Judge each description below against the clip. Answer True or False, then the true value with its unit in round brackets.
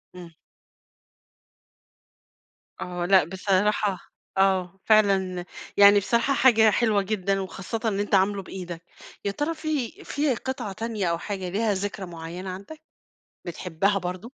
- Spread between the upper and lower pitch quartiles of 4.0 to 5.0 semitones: False (2.9 semitones)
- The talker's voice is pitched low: False (195 Hz)